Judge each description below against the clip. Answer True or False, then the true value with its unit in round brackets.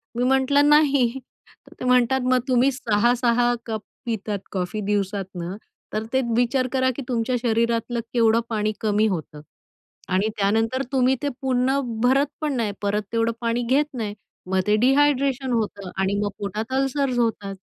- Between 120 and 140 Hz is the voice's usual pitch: False (235 Hz)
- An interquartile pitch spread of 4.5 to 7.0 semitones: False (3.7 semitones)